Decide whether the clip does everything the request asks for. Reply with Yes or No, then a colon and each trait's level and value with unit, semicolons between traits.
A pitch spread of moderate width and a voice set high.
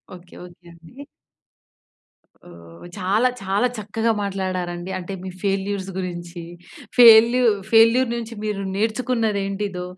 Yes: average, 3.8 semitones; high, 195 Hz